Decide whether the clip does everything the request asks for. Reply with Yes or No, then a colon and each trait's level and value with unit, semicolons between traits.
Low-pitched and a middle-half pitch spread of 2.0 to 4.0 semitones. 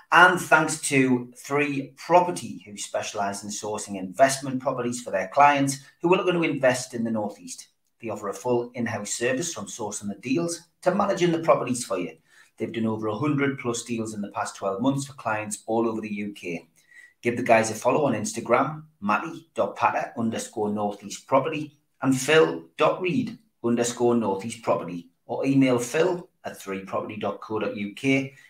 No: low, 120 Hz; average, 5.3 semitones